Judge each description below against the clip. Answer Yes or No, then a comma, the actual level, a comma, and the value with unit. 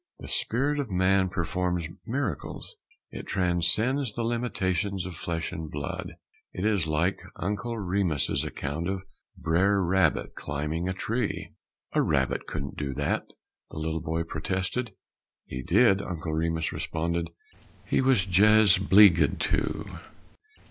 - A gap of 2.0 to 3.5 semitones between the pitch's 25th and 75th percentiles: No, average, 4.0 semitones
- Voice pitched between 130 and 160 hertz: No, very low, 90 Hz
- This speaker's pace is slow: Yes, slow, 130 wpm